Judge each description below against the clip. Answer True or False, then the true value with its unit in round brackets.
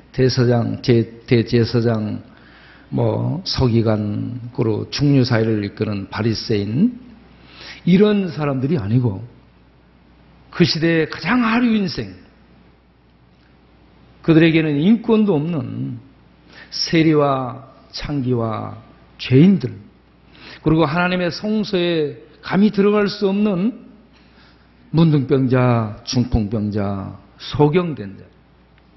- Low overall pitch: True (130 Hz)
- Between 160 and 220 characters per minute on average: True (195 characters per minute)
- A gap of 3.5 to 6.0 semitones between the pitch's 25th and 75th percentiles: False (7.4 semitones)